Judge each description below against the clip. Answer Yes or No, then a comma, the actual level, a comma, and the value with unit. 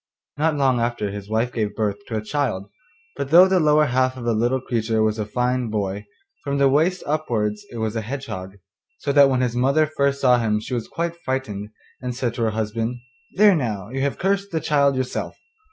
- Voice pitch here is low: Yes, low, 125 Hz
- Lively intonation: No, average, 4.4 semitones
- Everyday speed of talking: No, fast, 220 wpm